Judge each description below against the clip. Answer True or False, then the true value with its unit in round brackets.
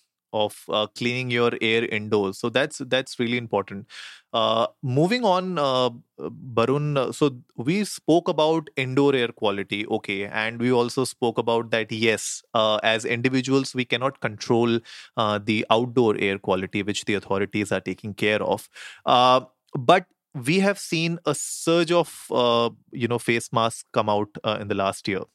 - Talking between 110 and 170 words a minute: True (165 wpm)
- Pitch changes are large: False (4.3 semitones)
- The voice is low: True (120 Hz)